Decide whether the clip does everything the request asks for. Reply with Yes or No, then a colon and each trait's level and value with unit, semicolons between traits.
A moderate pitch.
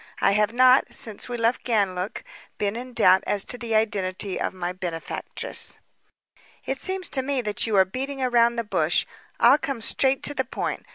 No: high, 230 Hz